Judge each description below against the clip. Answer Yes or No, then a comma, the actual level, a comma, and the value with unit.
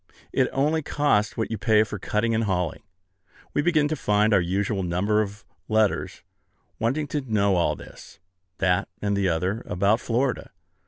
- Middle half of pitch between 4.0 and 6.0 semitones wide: No, average, 2.9 semitones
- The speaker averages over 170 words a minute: No, average, 165 wpm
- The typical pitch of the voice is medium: No, low, 105 Hz